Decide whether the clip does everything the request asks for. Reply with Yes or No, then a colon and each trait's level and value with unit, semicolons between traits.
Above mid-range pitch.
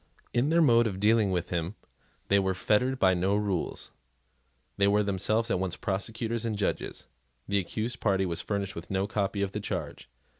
No: low, 100 Hz